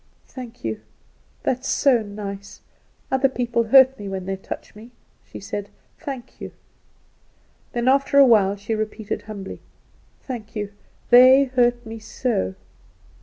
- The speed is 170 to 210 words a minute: No, average, 145 wpm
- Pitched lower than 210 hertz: No, high, 230 Hz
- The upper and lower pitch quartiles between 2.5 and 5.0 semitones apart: Yes, average, 4.0 semitones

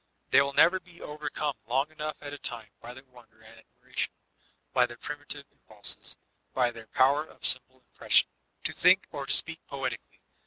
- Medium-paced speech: Yes, average, 180 wpm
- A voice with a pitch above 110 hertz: Yes, low, 135 Hz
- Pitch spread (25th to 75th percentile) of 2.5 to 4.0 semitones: Yes, average, 3.4 semitones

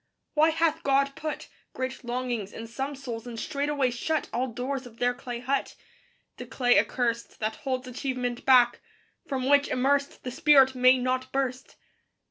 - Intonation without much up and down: Yes, narrow, 2.1 semitones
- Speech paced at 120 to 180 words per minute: Yes, average, 160 wpm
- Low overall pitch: No, very high, 255 Hz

